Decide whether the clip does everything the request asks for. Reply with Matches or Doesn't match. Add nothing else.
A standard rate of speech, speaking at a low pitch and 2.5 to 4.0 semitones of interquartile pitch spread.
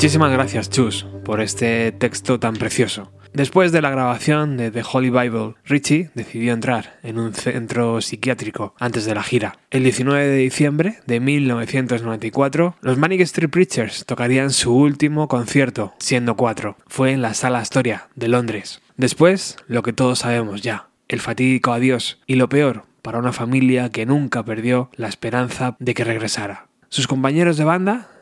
Matches